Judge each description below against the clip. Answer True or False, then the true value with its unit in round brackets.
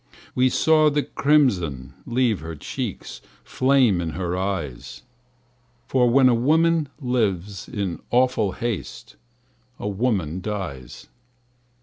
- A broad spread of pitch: True (6.2 semitones)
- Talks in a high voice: False (110 Hz)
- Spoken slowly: True (110 wpm)